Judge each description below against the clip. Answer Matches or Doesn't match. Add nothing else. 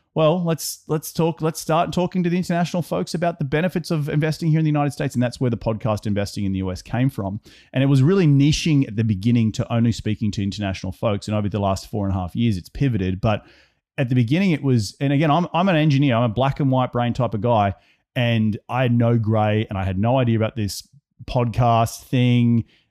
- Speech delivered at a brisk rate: Matches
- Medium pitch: Doesn't match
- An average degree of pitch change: Doesn't match